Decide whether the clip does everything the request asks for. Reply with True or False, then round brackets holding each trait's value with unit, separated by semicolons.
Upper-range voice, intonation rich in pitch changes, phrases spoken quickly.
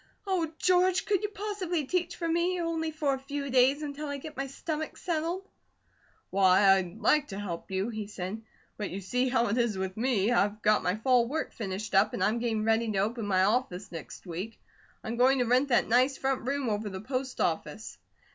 True (245 Hz; 6.5 semitones; 210 wpm)